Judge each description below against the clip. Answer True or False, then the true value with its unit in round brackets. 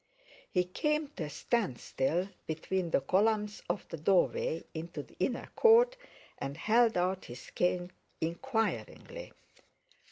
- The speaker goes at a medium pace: False (125 wpm)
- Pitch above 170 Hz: True (185 Hz)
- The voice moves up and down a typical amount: False (5.8 semitones)